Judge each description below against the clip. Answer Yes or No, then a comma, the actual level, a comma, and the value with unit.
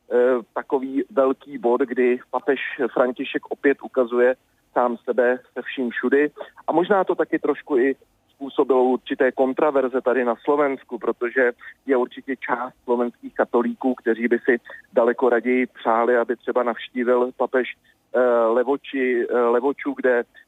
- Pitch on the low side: Yes, low, 125 Hz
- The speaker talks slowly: No, average, 130 wpm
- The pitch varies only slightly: Yes, narrow, 2.1 semitones